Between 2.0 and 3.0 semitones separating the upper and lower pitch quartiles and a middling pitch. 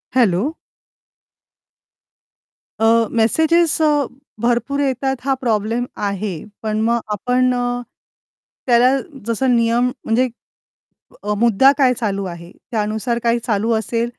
No: average, 2.7 semitones; high, 235 Hz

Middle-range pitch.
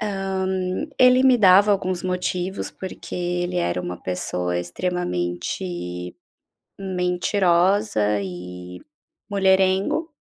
Yes: medium, 180 Hz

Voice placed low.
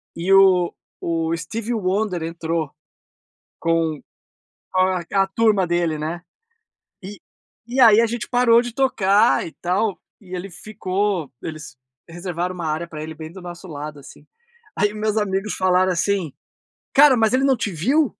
No: medium, 185 Hz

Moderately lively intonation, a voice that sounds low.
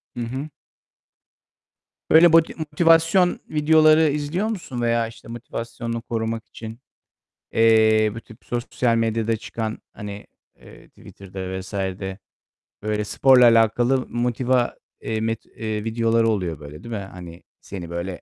Yes: average, 3.3 semitones; low, 115 Hz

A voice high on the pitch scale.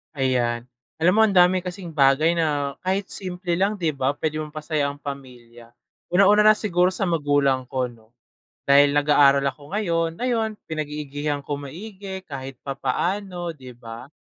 No: medium, 150 Hz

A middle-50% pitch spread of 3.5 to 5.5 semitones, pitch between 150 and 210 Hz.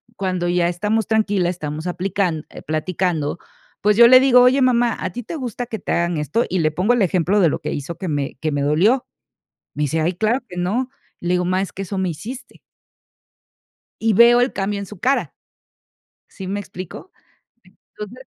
Yes: average, 5.0 semitones; high, 190 Hz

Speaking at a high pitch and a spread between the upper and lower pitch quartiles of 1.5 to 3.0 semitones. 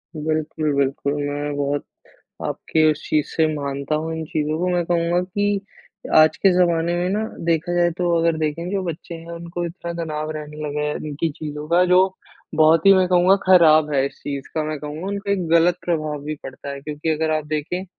No: medium, 160 Hz; narrow, 2.6 semitones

